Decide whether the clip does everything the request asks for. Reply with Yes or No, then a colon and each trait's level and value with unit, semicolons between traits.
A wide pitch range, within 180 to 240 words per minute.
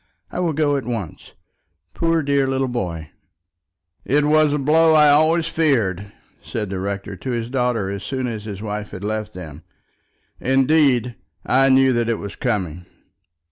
No: wide, 5.8 semitones; average, 165 wpm